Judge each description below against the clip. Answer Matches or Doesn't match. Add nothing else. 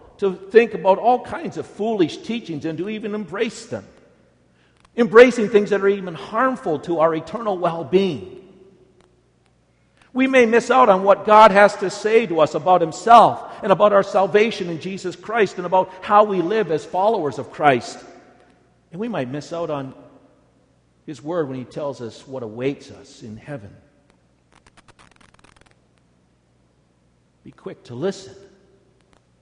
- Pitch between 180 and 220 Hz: Matches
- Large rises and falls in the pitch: Matches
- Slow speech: Doesn't match